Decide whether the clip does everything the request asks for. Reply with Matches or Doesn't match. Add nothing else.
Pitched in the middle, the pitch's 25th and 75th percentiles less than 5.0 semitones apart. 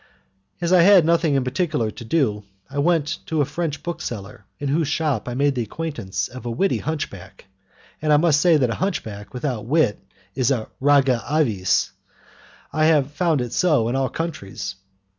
Doesn't match